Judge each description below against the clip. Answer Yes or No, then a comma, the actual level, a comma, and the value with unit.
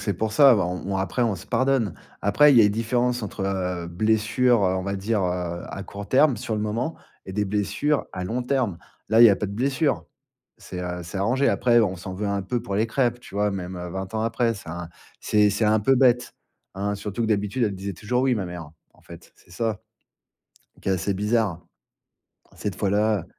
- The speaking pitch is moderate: No, low, 105 Hz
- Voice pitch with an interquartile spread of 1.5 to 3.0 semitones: No, average, 3.7 semitones